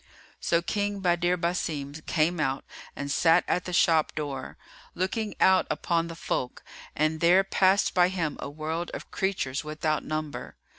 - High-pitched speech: No, medium, 165 Hz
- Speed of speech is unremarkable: Yes, average, 155 wpm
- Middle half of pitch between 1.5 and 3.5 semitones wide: Yes, average, 2.9 semitones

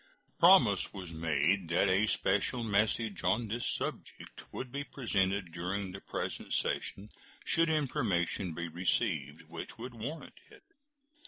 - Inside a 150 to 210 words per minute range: No, slow, 135 wpm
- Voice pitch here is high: No, low, 100 Hz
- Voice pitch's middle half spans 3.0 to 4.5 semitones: No, average, 5.1 semitones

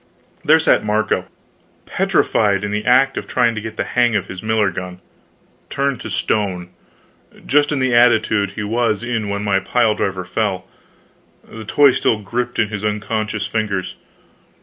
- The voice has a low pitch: Yes, low, 110 Hz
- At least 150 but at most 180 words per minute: Yes, average, 165 wpm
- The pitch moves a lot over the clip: No, average, 2.9 semitones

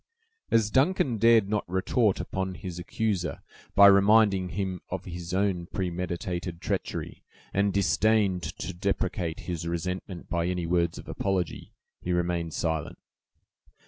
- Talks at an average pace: No, slow, 130 wpm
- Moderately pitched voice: No, very low, 95 Hz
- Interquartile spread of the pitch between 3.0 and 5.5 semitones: No, narrow, 2.5 semitones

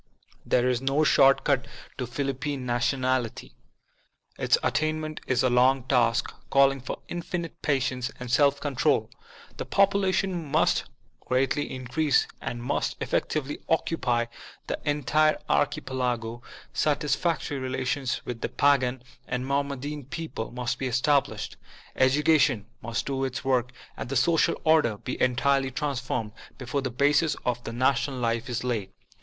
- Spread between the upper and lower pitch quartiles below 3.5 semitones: Yes, average, 2.7 semitones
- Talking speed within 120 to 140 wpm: Yes, slow, 135 wpm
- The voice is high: No, low, 130 Hz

